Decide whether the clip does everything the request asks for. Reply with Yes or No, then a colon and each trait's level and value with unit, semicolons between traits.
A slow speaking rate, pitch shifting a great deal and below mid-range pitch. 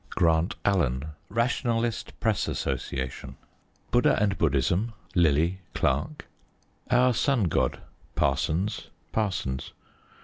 Yes: slow, 95 wpm; wide, 6.9 semitones; very low, 95 Hz